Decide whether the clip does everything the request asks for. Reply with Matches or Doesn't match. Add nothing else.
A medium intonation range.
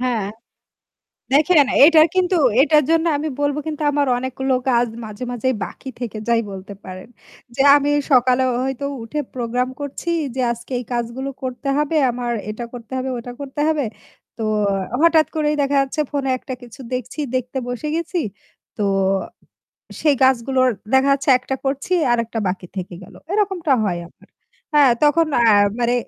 Matches